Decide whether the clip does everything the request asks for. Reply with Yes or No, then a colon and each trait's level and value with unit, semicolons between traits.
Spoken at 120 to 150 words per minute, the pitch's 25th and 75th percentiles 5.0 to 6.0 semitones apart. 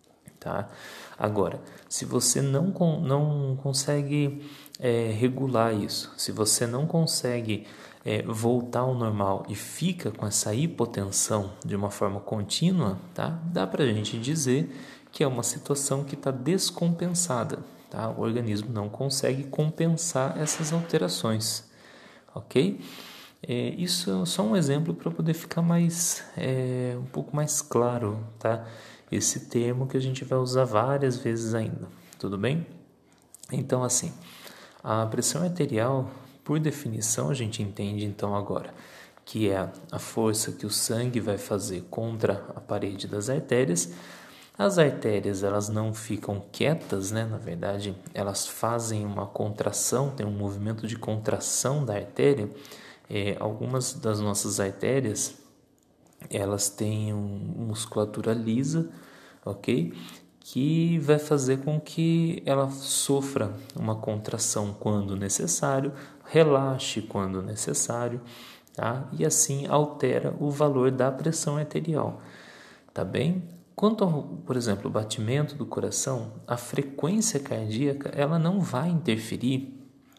Yes: average, 130 wpm; wide, 5.4 semitones